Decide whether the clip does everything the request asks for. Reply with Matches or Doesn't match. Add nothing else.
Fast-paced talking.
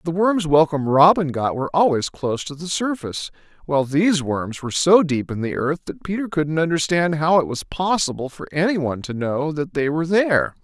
Matches